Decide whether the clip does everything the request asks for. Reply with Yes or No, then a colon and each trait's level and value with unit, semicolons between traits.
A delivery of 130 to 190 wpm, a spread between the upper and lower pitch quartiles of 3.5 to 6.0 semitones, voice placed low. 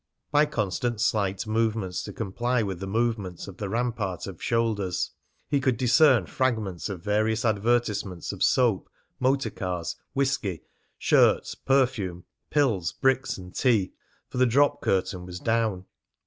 Yes: average, 140 wpm; average, 4.7 semitones; low, 110 Hz